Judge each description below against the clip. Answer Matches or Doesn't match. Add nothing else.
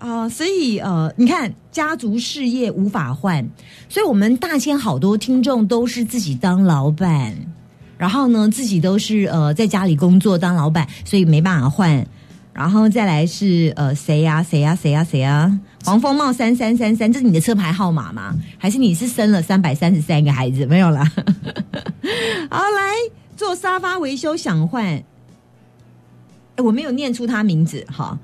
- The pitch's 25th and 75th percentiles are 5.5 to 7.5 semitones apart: Matches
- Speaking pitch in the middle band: Doesn't match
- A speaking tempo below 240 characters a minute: Doesn't match